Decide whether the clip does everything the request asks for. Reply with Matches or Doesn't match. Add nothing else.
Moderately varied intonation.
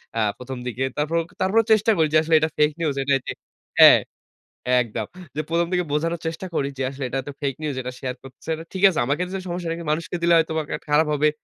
Matches